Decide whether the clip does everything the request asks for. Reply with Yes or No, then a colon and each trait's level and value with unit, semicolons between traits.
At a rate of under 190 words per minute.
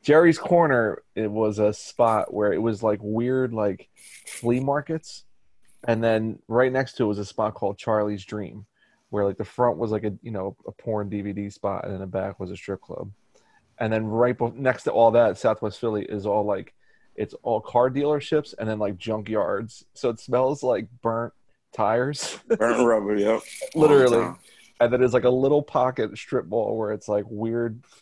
No: average, 195 wpm